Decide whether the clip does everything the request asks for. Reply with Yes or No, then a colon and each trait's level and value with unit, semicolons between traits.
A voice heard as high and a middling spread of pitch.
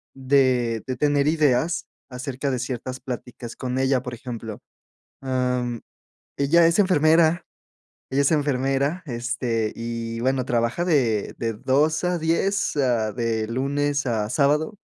No: low, 130 Hz; average, 3.4 semitones